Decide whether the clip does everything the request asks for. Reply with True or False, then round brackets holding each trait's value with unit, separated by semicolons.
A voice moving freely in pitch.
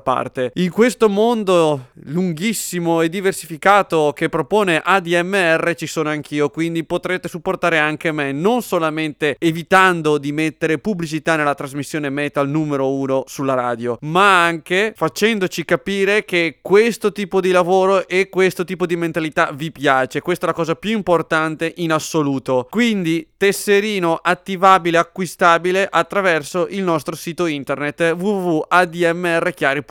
False (3.2 semitones)